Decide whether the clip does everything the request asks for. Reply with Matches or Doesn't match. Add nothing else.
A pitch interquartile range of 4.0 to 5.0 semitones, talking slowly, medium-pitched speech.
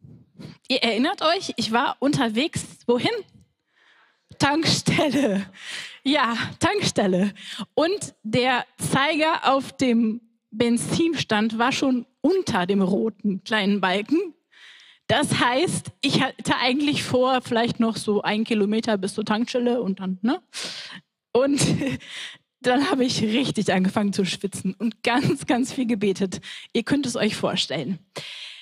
Doesn't match